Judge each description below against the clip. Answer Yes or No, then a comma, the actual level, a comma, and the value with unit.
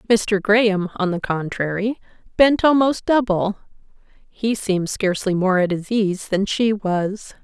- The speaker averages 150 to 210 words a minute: No, slow, 135 wpm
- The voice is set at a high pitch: Yes, high, 205 Hz